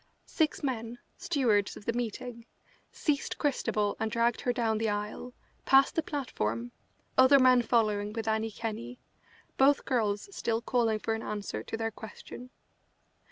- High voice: Yes, high, 230 Hz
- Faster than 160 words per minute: No, average, 150 wpm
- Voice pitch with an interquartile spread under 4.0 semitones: Yes, narrow, 2.6 semitones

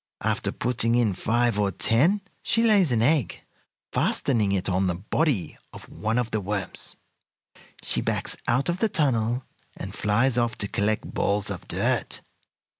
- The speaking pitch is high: No, low, 115 Hz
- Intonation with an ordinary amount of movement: Yes, average, 4.2 semitones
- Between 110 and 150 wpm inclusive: No, average, 160 wpm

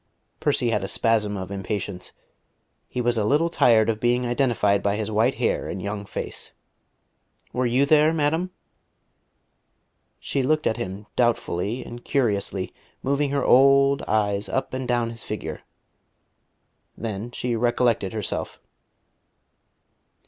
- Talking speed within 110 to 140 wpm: Yes, slow, 135 wpm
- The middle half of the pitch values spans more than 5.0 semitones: No, average, 4.1 semitones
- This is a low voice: Yes, low, 115 Hz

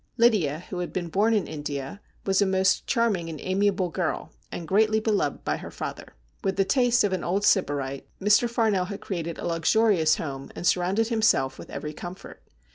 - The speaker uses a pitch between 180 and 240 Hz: Yes, high, 190 Hz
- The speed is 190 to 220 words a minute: Yes, average, 195 wpm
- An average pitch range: Yes, average, 4.4 semitones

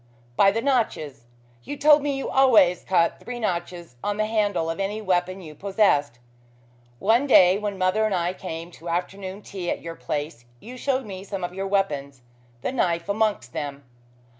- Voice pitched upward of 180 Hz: Yes, high, 190 Hz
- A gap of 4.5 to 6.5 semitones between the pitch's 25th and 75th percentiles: No, average, 4.1 semitones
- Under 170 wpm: No, average, 180 wpm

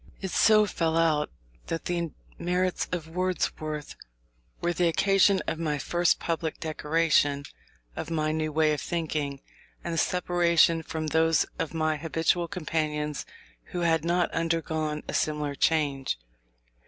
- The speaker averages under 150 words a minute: Yes, slow, 135 wpm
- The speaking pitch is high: No, medium, 160 Hz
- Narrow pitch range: Yes, narrow, 1.9 semitones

